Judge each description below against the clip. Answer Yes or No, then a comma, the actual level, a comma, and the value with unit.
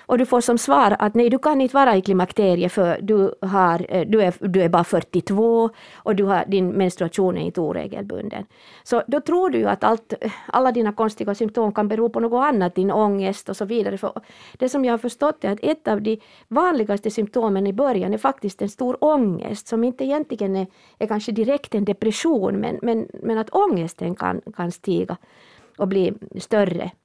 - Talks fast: Yes, fast, 200 wpm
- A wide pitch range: No, average, 3.8 semitones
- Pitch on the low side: No, high, 215 Hz